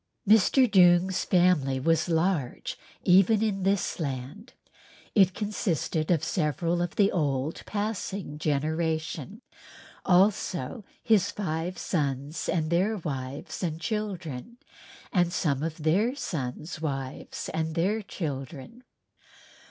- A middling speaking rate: No, slow, 110 wpm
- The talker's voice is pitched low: No, medium, 170 Hz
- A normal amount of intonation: Yes, average, 4.4 semitones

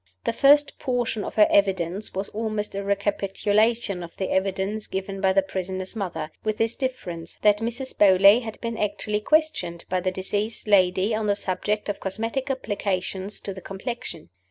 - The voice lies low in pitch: No, high, 200 Hz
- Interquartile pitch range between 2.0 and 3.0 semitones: Yes, average, 2.7 semitones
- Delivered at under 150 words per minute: No, average, 170 wpm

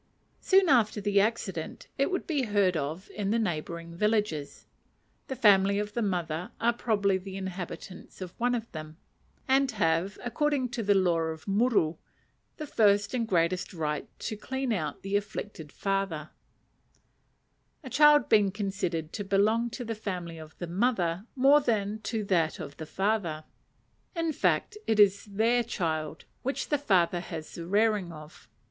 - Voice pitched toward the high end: Yes, high, 200 Hz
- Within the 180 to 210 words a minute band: No, average, 160 wpm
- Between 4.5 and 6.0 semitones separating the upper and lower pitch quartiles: Yes, average, 5.1 semitones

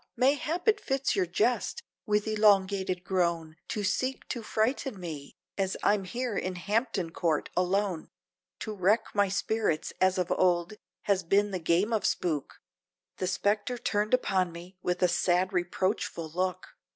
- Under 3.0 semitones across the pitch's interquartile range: No, average, 3.3 semitones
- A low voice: No, high, 190 Hz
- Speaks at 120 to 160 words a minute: Yes, average, 150 wpm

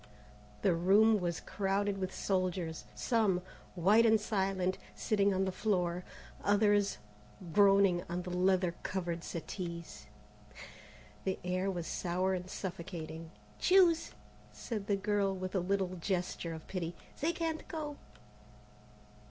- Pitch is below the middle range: No, high, 190 Hz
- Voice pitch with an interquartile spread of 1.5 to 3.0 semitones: Yes, narrow, 2.4 semitones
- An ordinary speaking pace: No, slow, 125 wpm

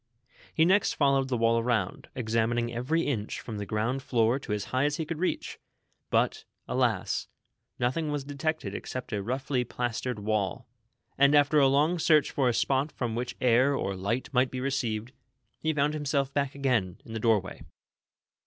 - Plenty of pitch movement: No, average, 3.8 semitones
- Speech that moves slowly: No, average, 175 wpm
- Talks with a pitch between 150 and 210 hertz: No, low, 130 Hz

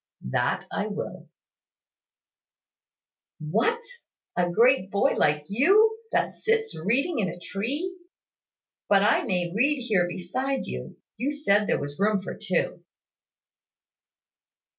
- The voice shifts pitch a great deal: Yes, wide, 7.5 semitones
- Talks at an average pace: No, slow, 120 wpm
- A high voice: Yes, high, 210 Hz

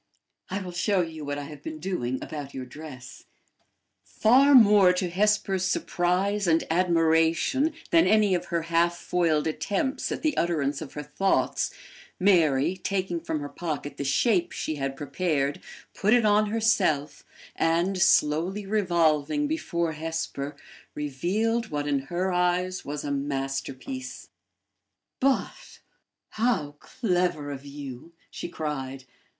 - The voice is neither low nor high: Yes, medium, 170 Hz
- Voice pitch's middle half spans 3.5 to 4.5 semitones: No, average, 5.1 semitones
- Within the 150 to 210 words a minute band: No, slow, 135 wpm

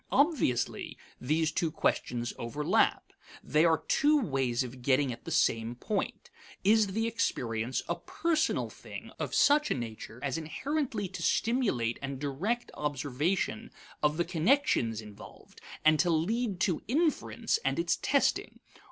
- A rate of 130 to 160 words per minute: Yes, average, 140 wpm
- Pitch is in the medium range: Yes, medium, 155 Hz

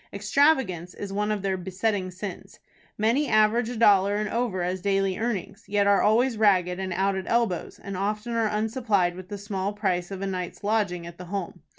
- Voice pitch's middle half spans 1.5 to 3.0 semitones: Yes, narrow, 2.6 semitones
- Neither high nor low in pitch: No, high, 200 Hz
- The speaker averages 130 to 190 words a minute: No, average, 200 wpm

